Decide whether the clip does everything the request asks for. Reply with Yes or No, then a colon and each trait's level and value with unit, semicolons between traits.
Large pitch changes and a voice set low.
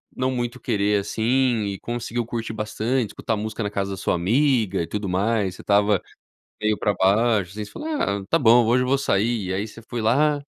No: average, 3.0 semitones; low, 110 Hz